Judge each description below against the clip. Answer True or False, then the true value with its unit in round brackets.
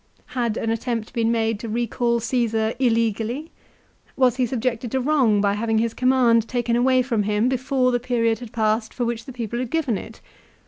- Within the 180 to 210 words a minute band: True (190 wpm)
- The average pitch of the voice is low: False (235 Hz)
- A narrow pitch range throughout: True (2.0 semitones)